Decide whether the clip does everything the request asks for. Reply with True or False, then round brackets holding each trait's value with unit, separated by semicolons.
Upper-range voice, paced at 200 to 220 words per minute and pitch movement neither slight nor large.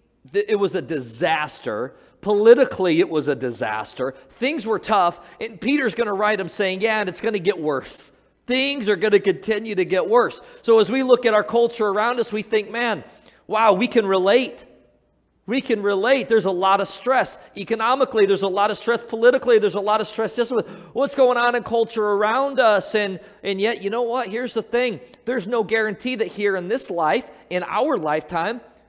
True (215 Hz; 205 wpm; 3.6 semitones)